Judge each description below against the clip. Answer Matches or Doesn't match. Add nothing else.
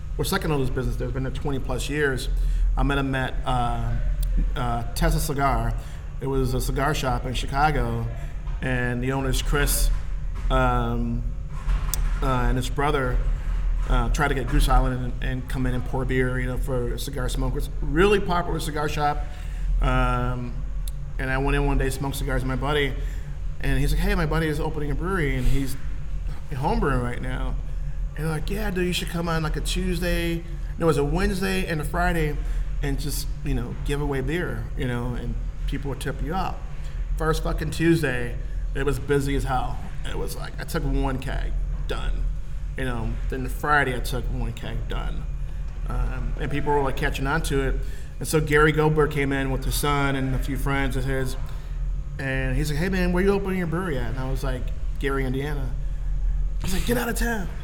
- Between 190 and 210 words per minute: Matches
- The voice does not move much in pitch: Doesn't match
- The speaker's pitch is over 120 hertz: Matches